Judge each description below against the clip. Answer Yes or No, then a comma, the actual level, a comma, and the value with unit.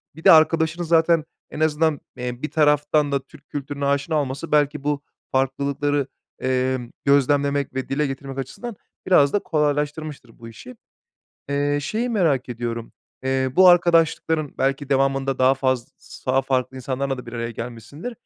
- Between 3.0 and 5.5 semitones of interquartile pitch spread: No, narrow, 2.5 semitones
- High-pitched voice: No, medium, 140 Hz